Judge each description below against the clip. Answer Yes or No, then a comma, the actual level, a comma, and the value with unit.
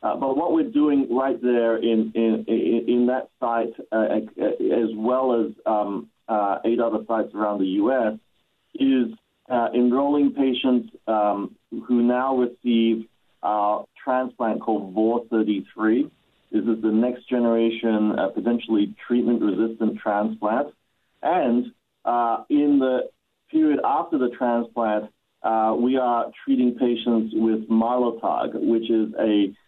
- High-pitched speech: No, low, 115 Hz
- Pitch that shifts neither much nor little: No, narrow, 2.1 semitones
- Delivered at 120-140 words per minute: Yes, slow, 135 wpm